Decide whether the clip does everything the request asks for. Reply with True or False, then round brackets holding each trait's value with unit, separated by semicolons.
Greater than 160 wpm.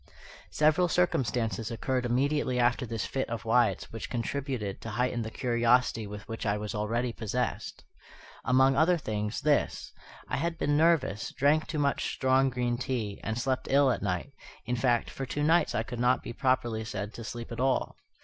True (180 wpm)